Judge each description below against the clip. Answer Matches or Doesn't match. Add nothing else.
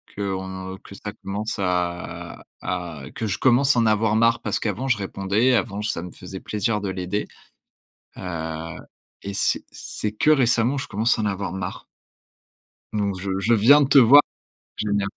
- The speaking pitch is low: Matches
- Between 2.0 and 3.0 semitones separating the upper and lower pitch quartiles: Doesn't match